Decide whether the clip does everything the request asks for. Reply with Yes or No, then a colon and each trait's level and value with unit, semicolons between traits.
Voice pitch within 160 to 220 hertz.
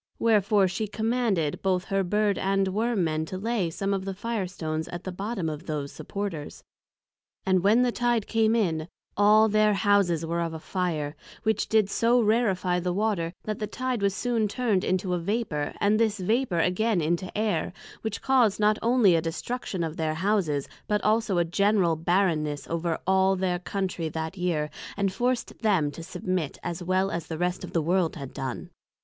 Yes: high, 190 Hz